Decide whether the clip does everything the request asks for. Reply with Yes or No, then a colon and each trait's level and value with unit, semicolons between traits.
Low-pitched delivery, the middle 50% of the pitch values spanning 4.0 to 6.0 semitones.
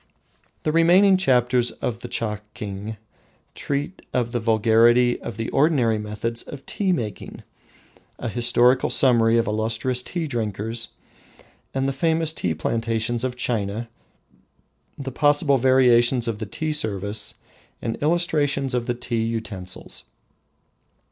No: low, 120 Hz; average, 3.3 semitones